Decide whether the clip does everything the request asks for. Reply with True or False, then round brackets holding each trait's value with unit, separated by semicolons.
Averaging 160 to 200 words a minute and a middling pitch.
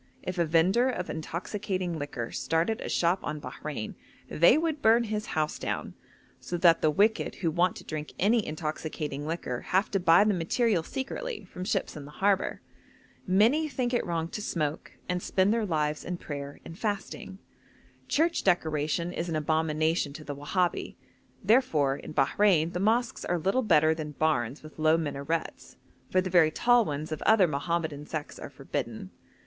True (175 wpm; 170 Hz)